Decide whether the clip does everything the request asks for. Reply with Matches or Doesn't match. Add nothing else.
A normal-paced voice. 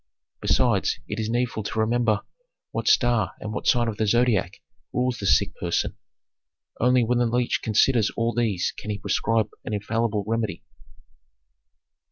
Matches